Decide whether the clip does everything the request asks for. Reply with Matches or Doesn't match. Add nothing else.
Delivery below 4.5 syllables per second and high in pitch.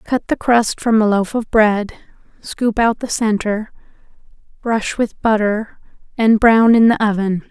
Matches